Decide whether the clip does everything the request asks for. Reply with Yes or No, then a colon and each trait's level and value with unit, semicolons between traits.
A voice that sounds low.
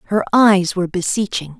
No: high, 190 Hz